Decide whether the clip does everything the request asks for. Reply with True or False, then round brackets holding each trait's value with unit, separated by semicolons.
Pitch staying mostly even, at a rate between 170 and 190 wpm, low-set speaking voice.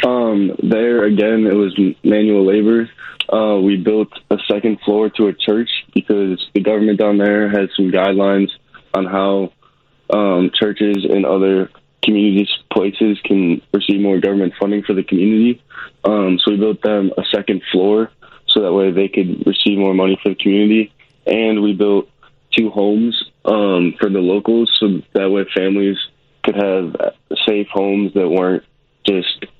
False (1.6 semitones; 160 wpm; 100 Hz)